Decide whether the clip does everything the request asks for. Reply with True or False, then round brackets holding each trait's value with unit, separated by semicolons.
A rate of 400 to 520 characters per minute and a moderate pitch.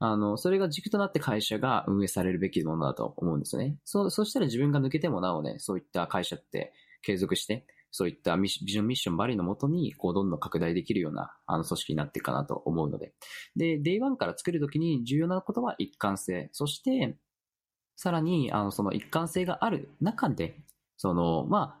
False (420 characters per minute; 130 Hz)